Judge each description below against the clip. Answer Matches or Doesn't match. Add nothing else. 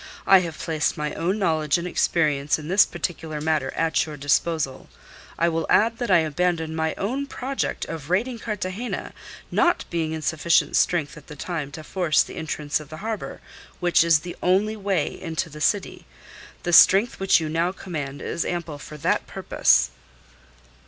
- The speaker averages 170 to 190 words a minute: Matches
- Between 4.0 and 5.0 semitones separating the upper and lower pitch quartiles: Doesn't match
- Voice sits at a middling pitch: Matches